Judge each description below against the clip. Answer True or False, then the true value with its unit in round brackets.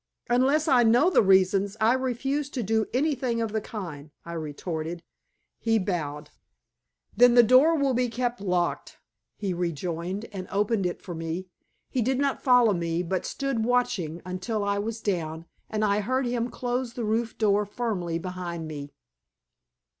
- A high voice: True (210 Hz)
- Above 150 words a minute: True (160 wpm)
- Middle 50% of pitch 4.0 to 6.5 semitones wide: True (5.6 semitones)